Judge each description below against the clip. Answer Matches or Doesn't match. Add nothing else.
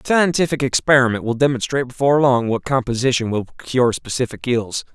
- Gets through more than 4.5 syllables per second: Matches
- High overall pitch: Doesn't match